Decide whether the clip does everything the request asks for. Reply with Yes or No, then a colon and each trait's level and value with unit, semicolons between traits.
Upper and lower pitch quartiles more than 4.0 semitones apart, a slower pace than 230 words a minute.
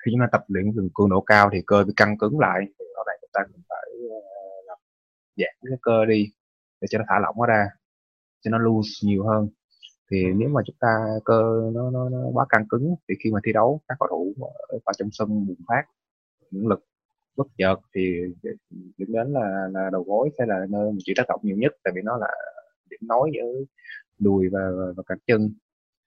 No: average, 3.7 semitones; average, 220 wpm